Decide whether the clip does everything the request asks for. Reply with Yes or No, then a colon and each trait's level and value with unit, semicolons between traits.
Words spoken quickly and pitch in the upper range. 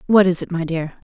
No: fast, 270 wpm; medium, 175 Hz